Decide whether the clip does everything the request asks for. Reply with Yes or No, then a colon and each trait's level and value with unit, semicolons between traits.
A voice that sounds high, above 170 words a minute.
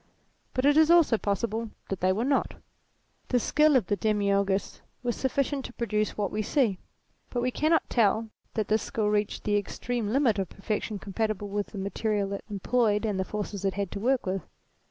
Yes: high, 215 Hz; average, 195 wpm